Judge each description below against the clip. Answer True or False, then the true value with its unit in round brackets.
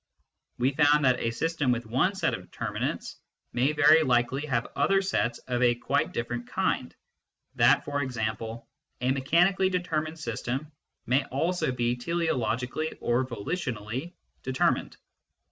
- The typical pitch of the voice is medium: False (130 Hz)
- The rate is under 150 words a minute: True (135 wpm)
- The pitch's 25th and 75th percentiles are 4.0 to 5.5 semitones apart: True (4.5 semitones)